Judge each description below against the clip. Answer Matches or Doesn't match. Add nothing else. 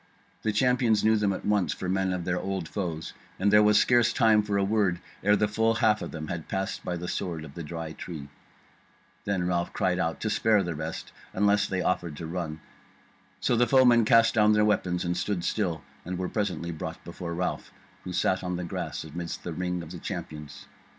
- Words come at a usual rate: Doesn't match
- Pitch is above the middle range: Doesn't match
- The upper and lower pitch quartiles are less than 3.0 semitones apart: Doesn't match